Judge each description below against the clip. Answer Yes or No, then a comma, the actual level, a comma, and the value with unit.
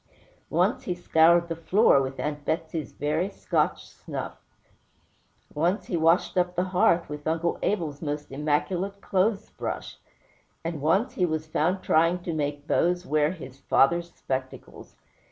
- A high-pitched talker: No, medium, 165 Hz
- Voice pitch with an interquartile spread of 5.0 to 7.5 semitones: No, average, 3.2 semitones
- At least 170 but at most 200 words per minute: No, average, 145 wpm